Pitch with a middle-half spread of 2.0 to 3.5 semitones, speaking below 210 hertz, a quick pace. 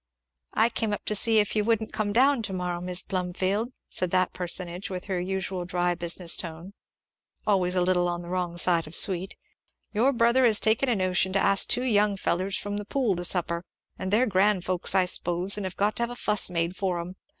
Yes: average, 2.9 semitones; high, 190 Hz; fast, 220 wpm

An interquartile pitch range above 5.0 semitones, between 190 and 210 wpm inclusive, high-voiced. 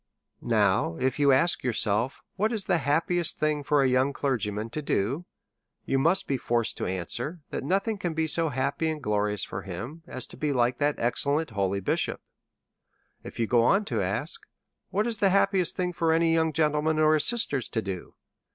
No: wide, 5.6 semitones; average, 195 wpm; medium, 145 Hz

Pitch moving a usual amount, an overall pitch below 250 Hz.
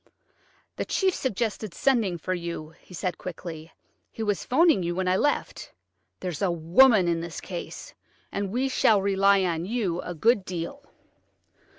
Yes: average, 4.6 semitones; medium, 185 Hz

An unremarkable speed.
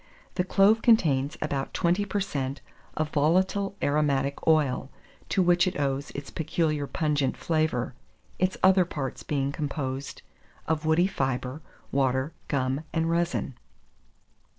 No: slow, 125 wpm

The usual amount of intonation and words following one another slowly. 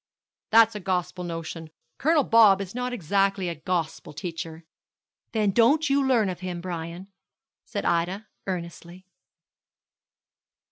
Yes: average, 4.5 semitones; slow, 125 wpm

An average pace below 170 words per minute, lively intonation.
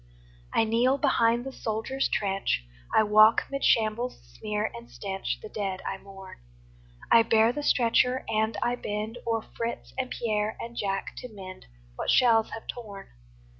No: average, 160 wpm; narrow, 2.6 semitones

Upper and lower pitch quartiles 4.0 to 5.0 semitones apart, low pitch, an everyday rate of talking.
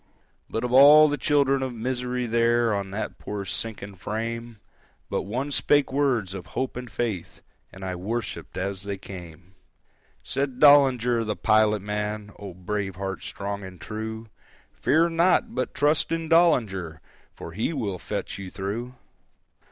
Yes: average, 4.7 semitones; low, 110 Hz; average, 145 wpm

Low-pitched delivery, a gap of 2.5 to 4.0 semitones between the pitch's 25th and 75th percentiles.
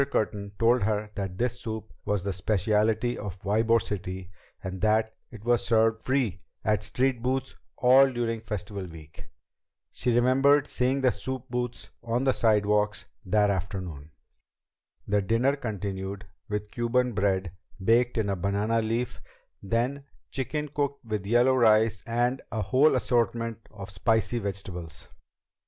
Yes: low, 110 Hz; average, 3.4 semitones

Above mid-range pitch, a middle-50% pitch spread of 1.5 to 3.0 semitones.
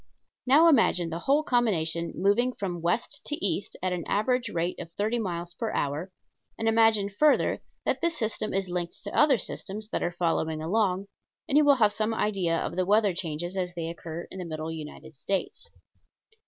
No: high, 195 Hz; average, 4.8 semitones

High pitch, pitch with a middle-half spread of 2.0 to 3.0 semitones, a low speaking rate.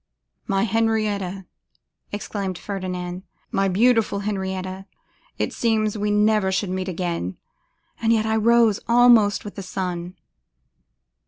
Yes: high, 200 Hz; average, 2.7 semitones; slow, 115 wpm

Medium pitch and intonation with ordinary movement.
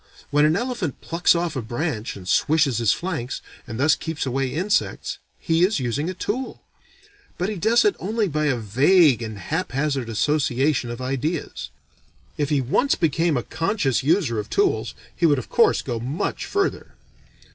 No: medium, 150 Hz; wide, 5.7 semitones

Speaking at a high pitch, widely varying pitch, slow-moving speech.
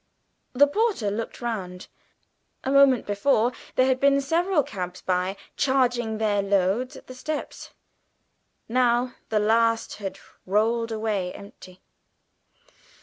No: high, 230 Hz; average, 4.3 semitones; slow, 115 wpm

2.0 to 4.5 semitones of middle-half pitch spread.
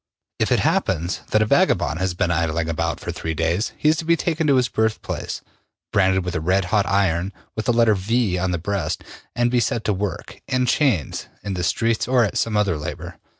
No: average, 4.9 semitones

